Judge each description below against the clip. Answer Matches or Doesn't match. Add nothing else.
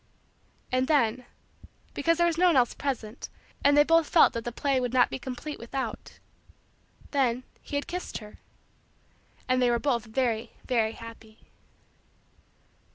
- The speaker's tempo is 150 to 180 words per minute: Matches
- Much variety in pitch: Doesn't match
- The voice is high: Matches